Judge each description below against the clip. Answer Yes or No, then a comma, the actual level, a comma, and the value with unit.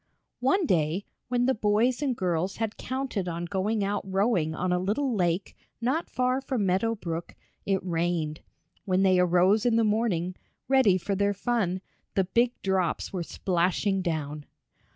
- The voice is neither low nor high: No, high, 195 Hz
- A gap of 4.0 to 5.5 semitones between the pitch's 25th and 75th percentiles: Yes, average, 4.4 semitones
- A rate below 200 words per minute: Yes, average, 160 wpm